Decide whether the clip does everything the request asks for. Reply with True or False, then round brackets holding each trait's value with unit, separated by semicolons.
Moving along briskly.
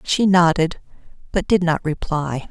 False (145 wpm)